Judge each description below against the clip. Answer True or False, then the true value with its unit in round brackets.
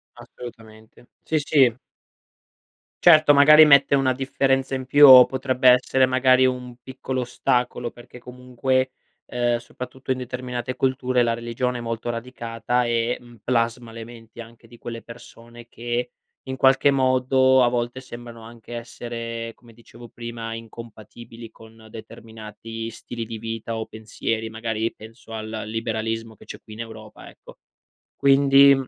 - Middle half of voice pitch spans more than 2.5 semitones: False (2.1 semitones)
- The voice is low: True (120 Hz)